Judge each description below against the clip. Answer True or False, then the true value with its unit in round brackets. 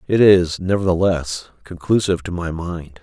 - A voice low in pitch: True (90 Hz)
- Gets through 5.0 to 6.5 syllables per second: False (4.7 syllables/s)